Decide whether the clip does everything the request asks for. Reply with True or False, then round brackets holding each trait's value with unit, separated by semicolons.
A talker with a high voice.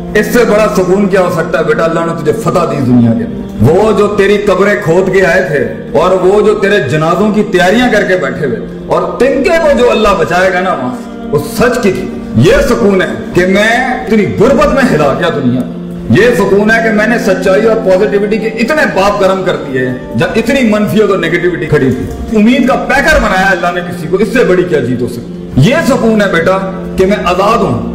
True (195 Hz)